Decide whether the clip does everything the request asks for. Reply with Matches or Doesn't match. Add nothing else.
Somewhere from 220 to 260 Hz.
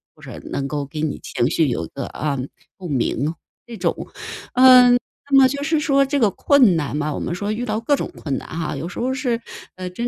Doesn't match